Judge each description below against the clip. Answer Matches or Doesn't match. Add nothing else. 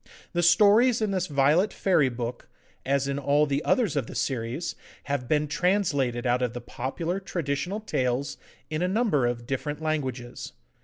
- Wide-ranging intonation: Matches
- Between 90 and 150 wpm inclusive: Doesn't match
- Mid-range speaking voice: Matches